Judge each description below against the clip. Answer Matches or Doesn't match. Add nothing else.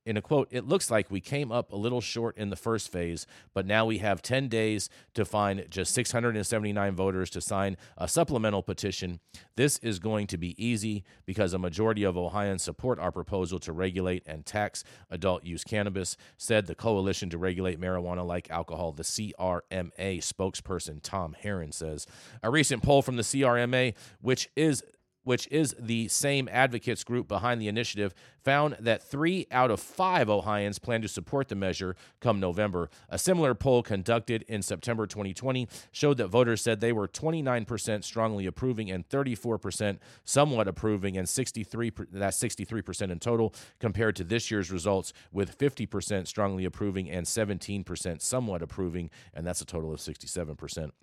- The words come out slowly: Doesn't match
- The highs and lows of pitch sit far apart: Doesn't match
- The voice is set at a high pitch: Doesn't match